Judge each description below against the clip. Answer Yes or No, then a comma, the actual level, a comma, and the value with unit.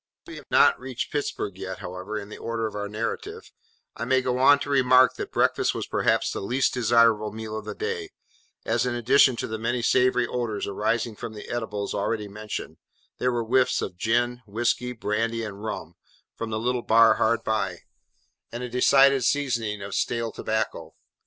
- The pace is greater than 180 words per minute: Yes, average, 190 wpm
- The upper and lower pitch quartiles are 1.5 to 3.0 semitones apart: Yes, average, 2.7 semitones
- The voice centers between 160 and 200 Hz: No, low, 115 Hz